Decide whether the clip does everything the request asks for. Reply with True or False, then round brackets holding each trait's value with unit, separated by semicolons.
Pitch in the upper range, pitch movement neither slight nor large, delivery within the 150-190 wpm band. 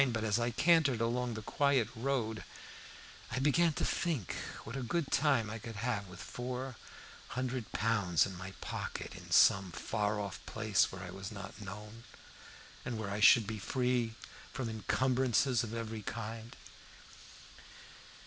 False (115 Hz; 3.3 semitones; 155 wpm)